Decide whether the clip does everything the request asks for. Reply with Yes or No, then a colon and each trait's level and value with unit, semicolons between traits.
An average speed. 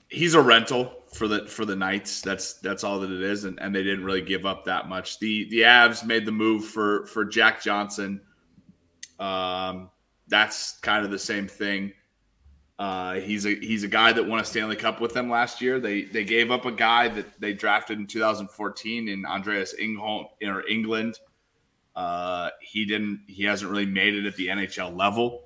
Yes: average, 195 wpm